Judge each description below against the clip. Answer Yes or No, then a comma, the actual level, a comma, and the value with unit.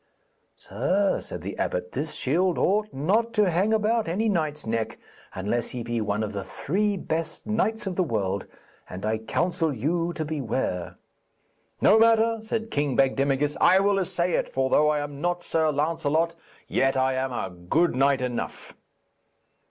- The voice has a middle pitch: Yes, medium, 155 Hz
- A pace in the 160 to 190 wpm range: Yes, average, 165 wpm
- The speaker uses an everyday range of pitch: No, wide, 6.9 semitones